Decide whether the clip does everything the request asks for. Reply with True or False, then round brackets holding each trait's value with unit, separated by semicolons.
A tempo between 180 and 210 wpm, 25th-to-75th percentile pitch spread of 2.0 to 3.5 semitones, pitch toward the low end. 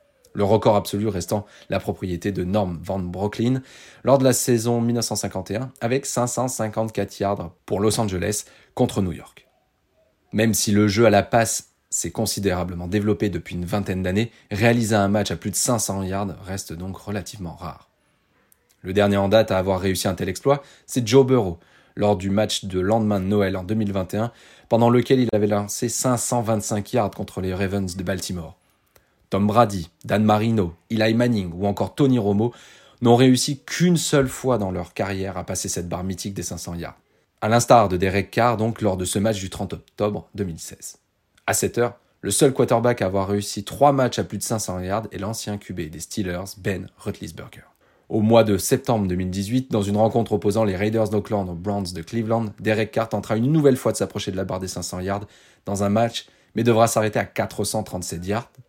True (190 wpm; 3.0 semitones; 105 Hz)